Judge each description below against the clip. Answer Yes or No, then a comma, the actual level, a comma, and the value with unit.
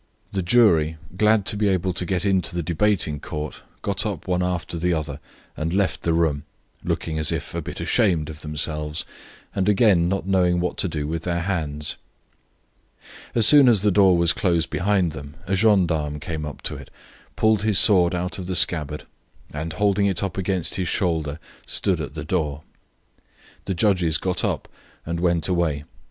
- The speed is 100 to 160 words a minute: No, average, 185 wpm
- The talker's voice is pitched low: Yes, very low, 90 Hz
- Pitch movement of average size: Yes, average, 3.6 semitones